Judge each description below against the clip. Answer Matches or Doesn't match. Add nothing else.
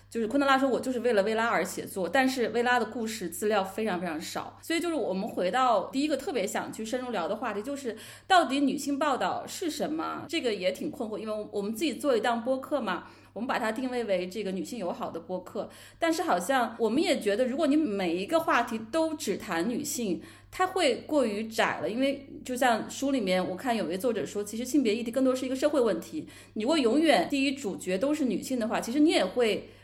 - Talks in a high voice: Matches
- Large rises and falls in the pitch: Doesn't match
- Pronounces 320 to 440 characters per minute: Matches